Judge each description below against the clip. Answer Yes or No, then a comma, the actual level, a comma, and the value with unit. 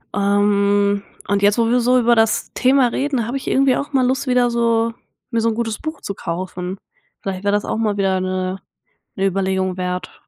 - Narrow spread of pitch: No, average, 3.8 semitones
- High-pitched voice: Yes, high, 210 Hz